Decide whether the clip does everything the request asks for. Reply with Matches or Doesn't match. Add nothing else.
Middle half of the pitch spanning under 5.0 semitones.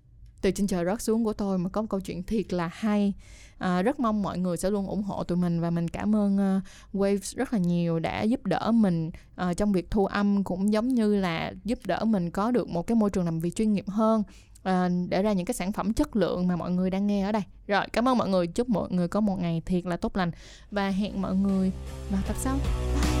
Matches